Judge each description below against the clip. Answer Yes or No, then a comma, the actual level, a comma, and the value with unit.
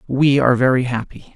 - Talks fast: No, average, 180 wpm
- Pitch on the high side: No, low, 130 Hz